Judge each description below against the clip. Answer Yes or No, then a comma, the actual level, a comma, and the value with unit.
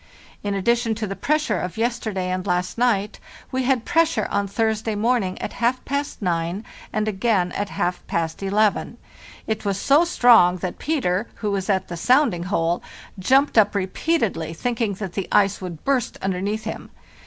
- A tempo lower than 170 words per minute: No, average, 175 wpm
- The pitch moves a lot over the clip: No, average, 4.5 semitones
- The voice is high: Yes, high, 205 Hz